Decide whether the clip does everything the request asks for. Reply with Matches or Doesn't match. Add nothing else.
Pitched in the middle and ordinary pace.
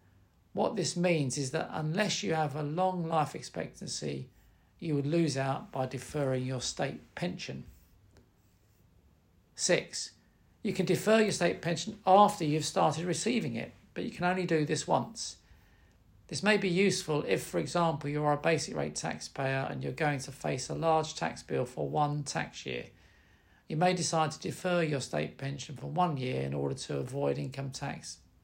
Matches